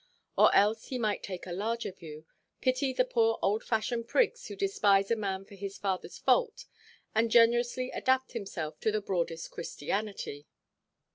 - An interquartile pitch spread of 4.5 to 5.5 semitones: No, average, 3.8 semitones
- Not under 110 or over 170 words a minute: Yes, average, 155 wpm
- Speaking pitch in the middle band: No, high, 215 Hz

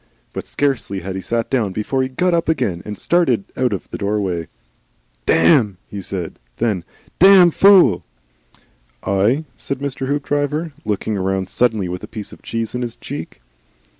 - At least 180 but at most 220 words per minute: No, average, 165 wpm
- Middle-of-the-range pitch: No, low, 115 Hz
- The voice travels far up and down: Yes, wide, 6.6 semitones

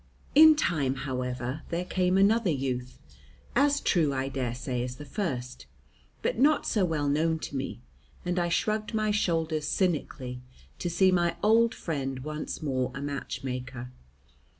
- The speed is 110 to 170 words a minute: Yes, average, 150 wpm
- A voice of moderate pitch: Yes, medium, 155 Hz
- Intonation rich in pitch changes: Yes, wide, 6.0 semitones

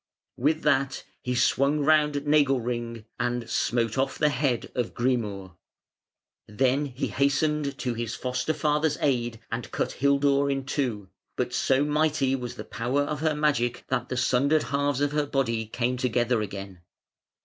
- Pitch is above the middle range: No, low, 135 Hz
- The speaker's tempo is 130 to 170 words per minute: Yes, average, 155 wpm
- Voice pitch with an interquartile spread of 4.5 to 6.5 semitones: No, average, 3.2 semitones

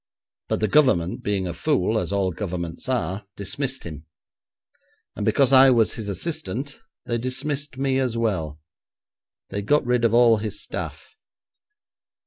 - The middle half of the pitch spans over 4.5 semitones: Yes, wide, 5.6 semitones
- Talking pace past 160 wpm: No, average, 145 wpm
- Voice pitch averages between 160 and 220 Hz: No, low, 115 Hz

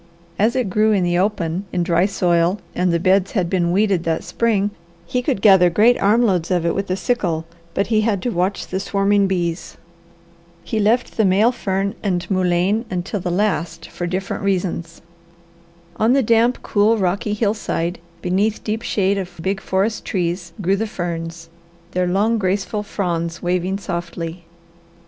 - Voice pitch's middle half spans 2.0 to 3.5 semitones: Yes, average, 3.1 semitones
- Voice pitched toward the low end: No, high, 190 Hz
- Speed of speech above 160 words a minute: Yes, average, 170 wpm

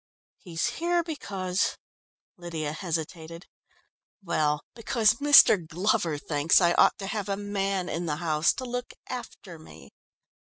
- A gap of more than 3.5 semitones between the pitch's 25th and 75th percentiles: Yes, average, 4.9 semitones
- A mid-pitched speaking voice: Yes, medium, 180 Hz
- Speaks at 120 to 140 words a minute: Yes, slow, 135 wpm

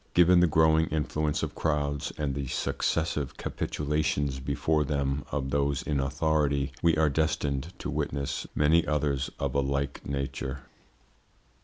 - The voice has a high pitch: No, very low, 75 Hz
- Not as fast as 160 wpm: Yes, average, 140 wpm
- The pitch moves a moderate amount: No, narrow, 2.0 semitones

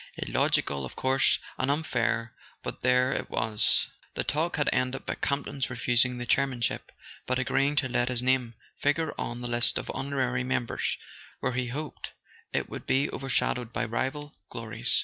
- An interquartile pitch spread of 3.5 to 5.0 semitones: No, narrow, 2.4 semitones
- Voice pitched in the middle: No, low, 130 Hz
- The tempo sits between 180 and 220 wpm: No, average, 165 wpm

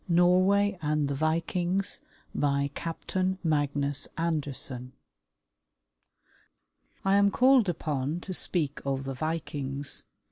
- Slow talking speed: Yes, slow, 100 wpm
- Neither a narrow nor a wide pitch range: Yes, average, 4.4 semitones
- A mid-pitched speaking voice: Yes, medium, 155 Hz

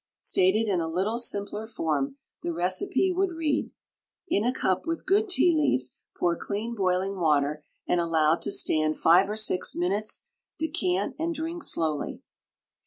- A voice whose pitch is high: Yes, high, 195 Hz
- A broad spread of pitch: Yes, wide, 8.3 semitones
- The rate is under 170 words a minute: Yes, average, 155 wpm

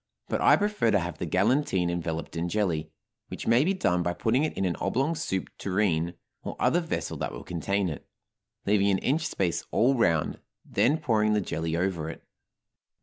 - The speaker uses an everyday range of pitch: No, wide, 5.9 semitones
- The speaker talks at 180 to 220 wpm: Yes, average, 190 wpm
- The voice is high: No, very low, 95 Hz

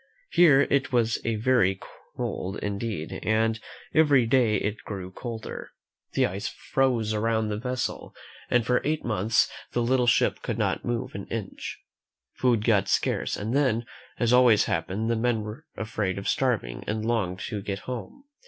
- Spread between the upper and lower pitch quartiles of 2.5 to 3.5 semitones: Yes, average, 3.0 semitones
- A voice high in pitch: No, low, 115 Hz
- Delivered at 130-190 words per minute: Yes, average, 160 wpm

